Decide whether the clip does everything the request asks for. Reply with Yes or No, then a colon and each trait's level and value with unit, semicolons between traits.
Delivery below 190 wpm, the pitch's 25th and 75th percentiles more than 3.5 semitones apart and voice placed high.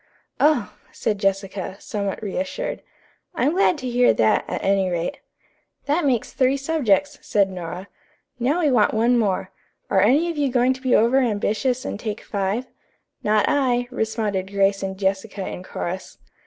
Yes: average, 160 wpm; average, 5.1 semitones; high, 220 Hz